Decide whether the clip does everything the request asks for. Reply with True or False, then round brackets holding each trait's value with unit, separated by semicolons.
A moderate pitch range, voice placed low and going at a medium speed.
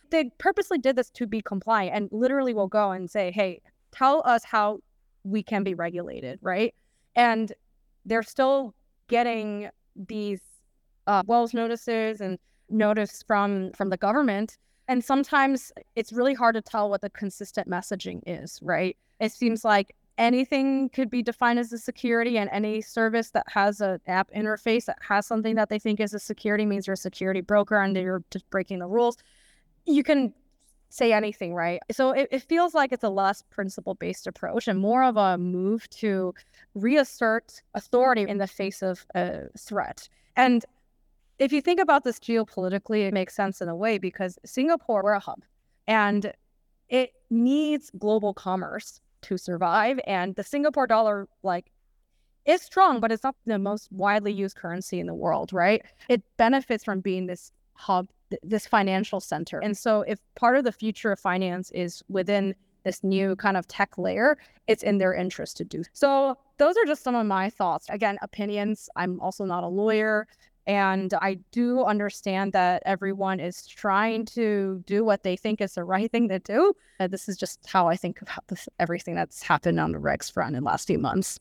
False (3.6 semitones; 210 Hz; 185 wpm)